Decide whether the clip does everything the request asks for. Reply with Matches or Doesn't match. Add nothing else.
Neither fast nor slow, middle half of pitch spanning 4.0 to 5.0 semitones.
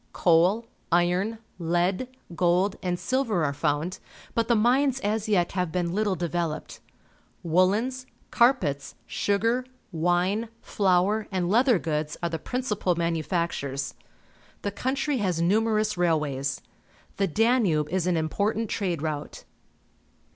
Doesn't match